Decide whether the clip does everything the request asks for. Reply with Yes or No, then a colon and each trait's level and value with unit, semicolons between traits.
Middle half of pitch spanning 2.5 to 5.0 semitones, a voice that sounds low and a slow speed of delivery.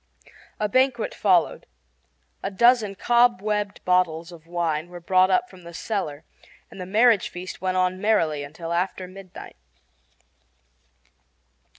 No: average, 3.4 semitones; medium, 185 Hz; slow, 125 wpm